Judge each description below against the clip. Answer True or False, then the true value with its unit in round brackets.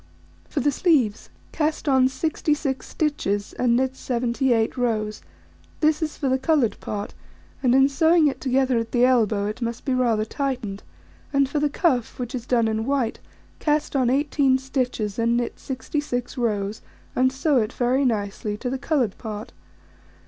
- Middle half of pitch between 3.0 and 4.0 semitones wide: True (3.4 semitones)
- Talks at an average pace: True (165 wpm)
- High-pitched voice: True (255 Hz)